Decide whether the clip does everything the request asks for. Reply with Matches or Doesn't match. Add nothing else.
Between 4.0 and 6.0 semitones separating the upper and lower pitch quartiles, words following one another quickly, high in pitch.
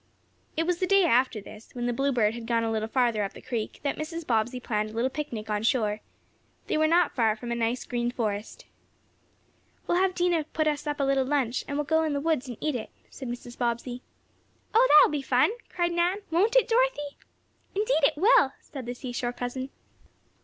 Matches